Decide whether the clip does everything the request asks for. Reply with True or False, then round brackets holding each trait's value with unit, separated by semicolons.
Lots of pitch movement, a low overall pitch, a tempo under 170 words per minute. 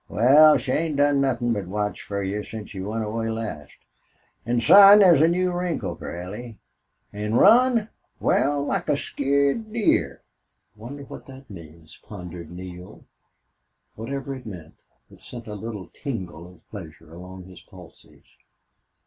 True (7.2 semitones; 115 Hz; 150 wpm)